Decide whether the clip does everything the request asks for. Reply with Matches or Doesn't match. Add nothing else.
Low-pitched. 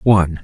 Matches